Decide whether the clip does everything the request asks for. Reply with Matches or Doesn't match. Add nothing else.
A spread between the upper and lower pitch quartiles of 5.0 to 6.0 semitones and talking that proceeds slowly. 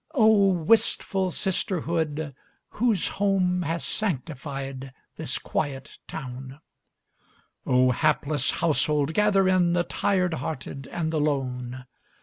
Matches